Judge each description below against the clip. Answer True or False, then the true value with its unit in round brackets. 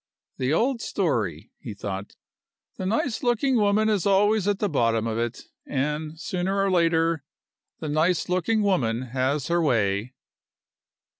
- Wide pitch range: True (8.0 semitones)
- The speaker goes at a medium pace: True (145 wpm)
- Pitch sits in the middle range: True (165 Hz)